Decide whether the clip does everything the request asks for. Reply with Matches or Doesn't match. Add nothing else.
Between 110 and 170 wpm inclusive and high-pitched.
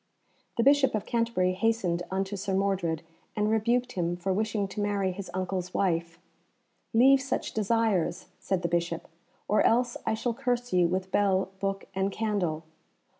Matches